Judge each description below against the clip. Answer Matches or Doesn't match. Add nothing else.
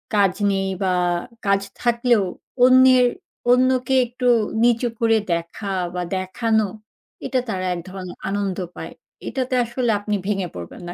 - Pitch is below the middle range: Doesn't match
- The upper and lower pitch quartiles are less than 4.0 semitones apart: Doesn't match